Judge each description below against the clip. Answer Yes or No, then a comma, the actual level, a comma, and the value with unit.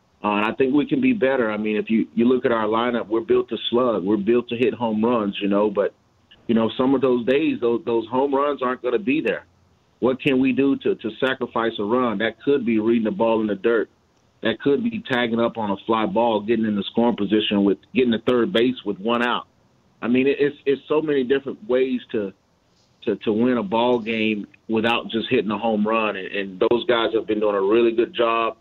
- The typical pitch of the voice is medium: No, low, 115 Hz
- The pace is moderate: No, fast, 245 wpm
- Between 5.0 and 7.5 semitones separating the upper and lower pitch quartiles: No, average, 2.8 semitones